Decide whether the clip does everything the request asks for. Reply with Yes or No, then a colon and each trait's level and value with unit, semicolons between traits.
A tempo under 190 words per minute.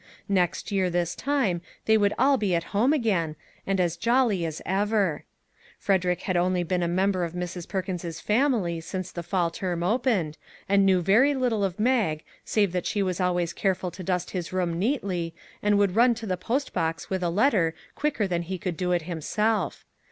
No: average, 195 wpm